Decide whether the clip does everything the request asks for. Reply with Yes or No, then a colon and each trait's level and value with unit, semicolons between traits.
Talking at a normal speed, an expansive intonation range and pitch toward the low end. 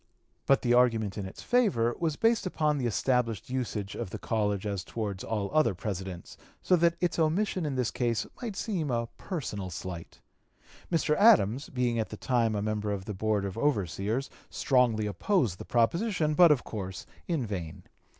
Yes: average, 180 wpm; wide, 6.8 semitones; low, 115 Hz